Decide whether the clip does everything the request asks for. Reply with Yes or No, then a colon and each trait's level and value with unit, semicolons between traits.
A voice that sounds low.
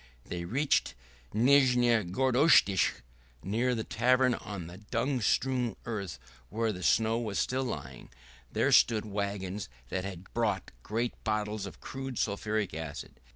Yes: low, 110 Hz